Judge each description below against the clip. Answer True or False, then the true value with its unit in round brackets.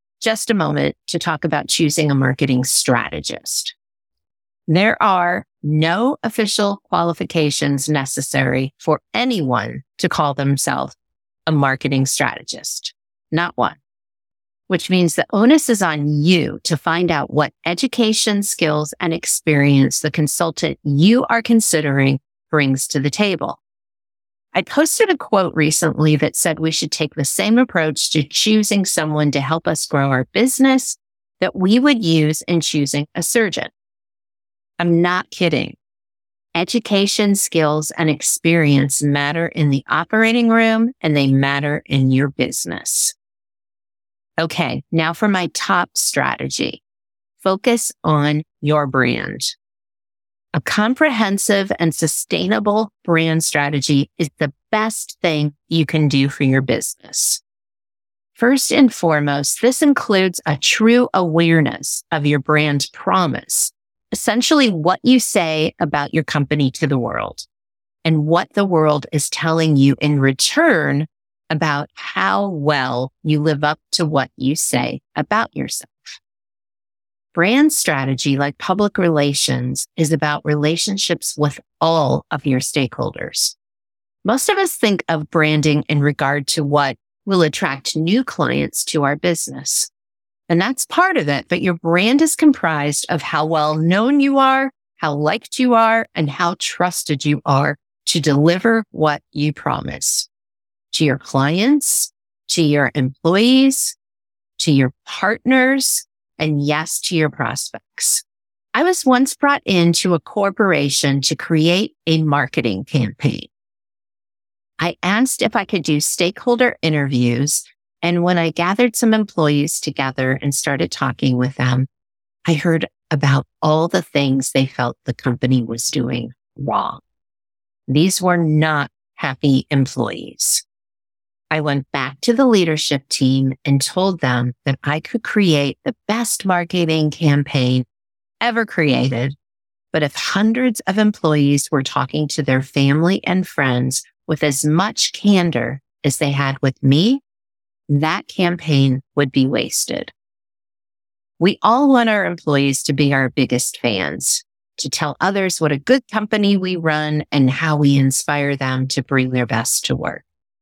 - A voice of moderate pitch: True (155 Hz)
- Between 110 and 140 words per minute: True (135 wpm)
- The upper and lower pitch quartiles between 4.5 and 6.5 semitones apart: True (5.2 semitones)